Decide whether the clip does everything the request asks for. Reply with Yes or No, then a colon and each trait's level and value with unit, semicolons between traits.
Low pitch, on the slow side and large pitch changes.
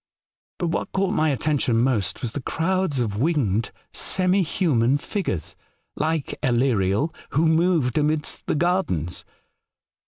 No: medium, 150 Hz; slow, 125 wpm; wide, 6.1 semitones